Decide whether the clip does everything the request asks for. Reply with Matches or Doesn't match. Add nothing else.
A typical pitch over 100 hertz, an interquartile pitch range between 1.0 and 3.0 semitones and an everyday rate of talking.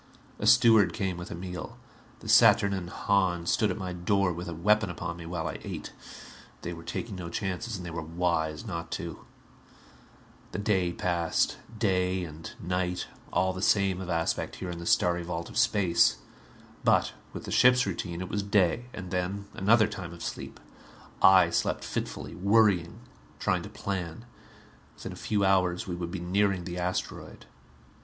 Doesn't match